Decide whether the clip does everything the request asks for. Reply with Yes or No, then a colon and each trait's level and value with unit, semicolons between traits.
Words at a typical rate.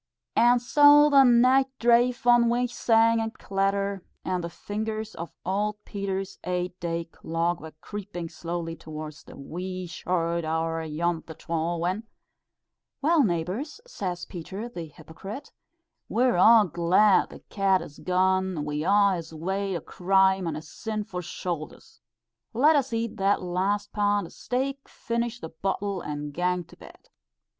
Yes: average, 150 wpm